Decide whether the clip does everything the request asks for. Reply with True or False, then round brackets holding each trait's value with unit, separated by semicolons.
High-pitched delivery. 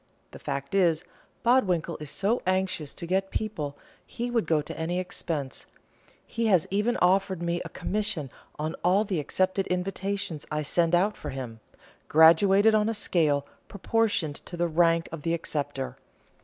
False (175 Hz)